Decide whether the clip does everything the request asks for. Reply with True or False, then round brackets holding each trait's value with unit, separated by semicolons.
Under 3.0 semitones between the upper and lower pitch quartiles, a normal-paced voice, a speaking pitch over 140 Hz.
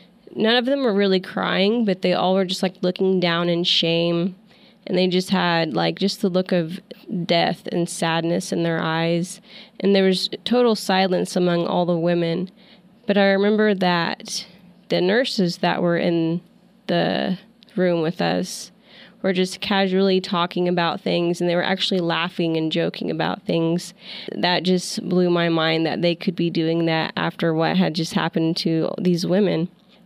True (2.5 semitones; 175 wpm; 185 Hz)